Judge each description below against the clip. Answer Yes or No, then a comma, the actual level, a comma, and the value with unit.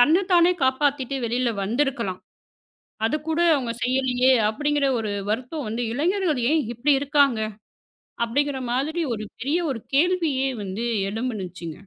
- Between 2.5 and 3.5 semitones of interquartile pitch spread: No, average, 4.2 semitones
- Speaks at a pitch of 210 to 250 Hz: No, very high, 265 Hz